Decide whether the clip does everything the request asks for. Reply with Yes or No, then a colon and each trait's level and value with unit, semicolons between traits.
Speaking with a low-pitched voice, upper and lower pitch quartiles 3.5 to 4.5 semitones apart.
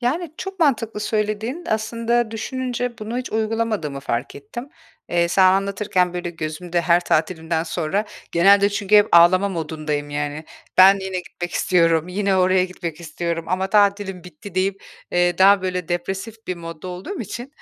No: medium, 185 Hz; average, 3.9 semitones